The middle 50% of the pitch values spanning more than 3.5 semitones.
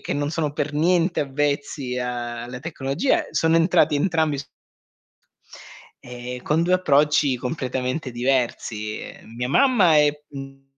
Yes: average, 4.0 semitones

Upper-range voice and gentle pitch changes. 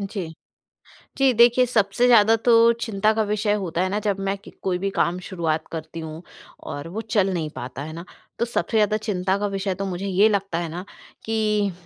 No: high, 195 Hz; average, 3.5 semitones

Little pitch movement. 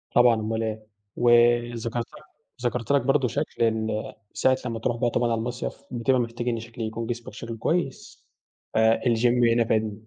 Yes: narrow, 1.4 semitones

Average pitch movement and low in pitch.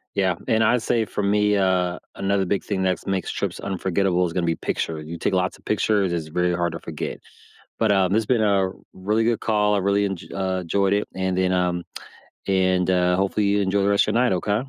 No: narrow, 2.2 semitones; very low, 95 Hz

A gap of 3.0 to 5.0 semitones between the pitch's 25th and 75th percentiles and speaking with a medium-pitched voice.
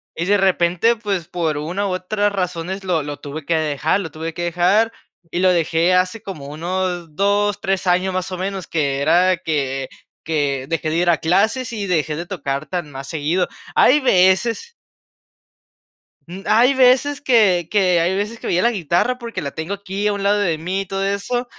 Yes: average, 3.8 semitones; medium, 180 Hz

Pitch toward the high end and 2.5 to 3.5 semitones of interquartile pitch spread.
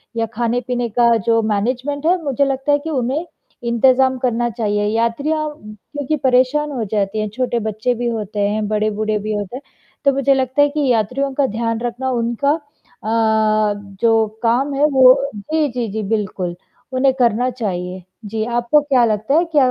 No: high, 240 Hz; average, 3.9 semitones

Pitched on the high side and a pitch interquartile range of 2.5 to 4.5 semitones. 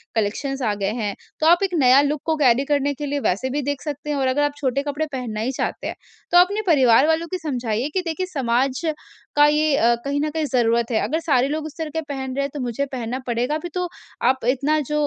Yes: very high, 280 Hz; average, 3.4 semitones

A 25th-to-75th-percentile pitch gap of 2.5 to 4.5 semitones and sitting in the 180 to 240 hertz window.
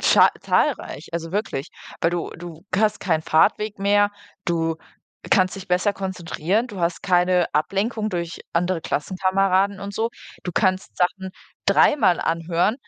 Yes: average, 2.9 semitones; medium, 185 Hz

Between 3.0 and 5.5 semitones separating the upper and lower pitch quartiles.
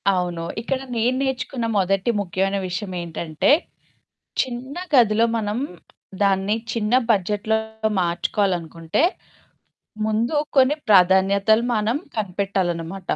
Yes: average, 3.8 semitones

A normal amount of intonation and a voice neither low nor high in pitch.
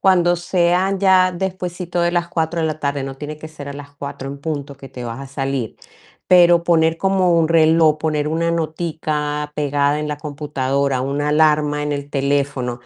Yes: average, 3.2 semitones; medium, 150 Hz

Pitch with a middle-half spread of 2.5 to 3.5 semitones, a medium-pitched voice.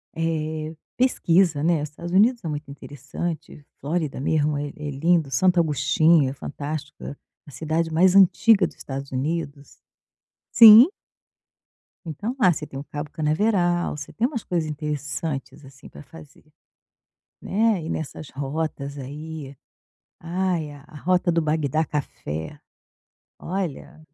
Yes: average, 3.1 semitones; medium, 155 Hz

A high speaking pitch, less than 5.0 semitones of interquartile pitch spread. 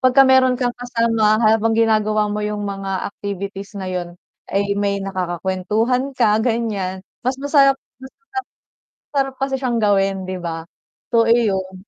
Yes: high, 210 Hz; average, 3.9 semitones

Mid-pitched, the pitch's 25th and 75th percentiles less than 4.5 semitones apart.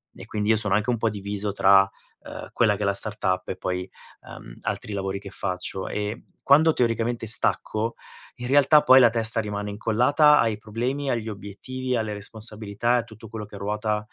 No: low, 110 Hz; narrow, 2.5 semitones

